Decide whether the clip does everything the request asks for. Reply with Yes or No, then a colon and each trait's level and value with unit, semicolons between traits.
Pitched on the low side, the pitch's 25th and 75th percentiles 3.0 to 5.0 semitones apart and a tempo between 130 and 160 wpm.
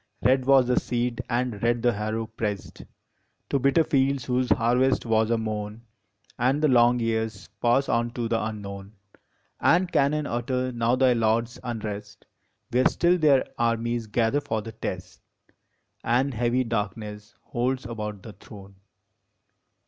No: low, 120 Hz; narrow, 2.5 semitones; average, 145 wpm